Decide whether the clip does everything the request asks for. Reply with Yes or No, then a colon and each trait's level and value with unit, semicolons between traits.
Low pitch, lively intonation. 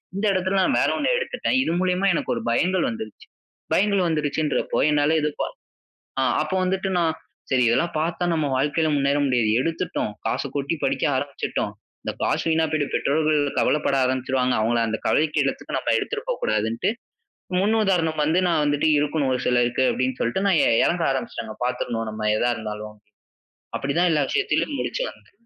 No: medium, 150 Hz; wide, 5.8 semitones